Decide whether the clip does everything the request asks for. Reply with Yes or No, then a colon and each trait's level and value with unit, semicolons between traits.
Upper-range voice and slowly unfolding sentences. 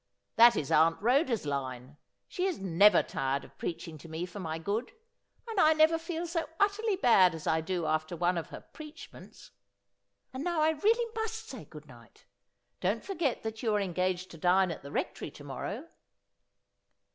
No: high, 200 Hz; average, 180 wpm